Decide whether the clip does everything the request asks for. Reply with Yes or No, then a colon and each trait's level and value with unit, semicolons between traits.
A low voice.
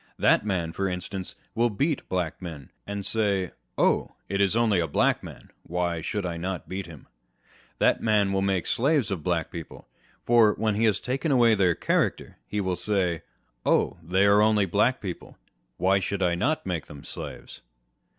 Yes: very low, 95 Hz